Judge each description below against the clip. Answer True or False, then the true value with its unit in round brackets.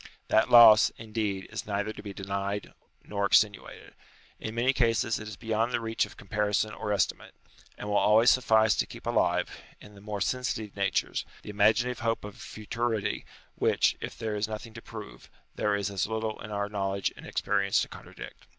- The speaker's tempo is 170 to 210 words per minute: True (195 wpm)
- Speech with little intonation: True (1.7 semitones)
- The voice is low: True (105 Hz)